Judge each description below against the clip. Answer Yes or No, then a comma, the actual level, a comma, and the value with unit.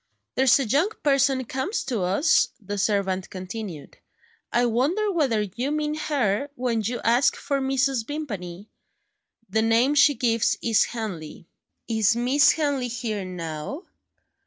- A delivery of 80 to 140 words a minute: Yes, slow, 135 wpm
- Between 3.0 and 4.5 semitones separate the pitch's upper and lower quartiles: No, average, 5.1 semitones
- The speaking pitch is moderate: No, high, 240 Hz